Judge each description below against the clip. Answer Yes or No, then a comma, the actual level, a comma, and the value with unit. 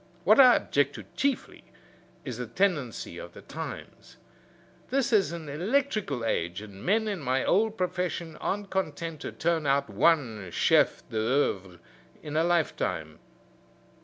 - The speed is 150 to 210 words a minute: No, average, 140 wpm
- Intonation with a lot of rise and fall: Yes, wide, 7.9 semitones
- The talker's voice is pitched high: No, medium, 160 Hz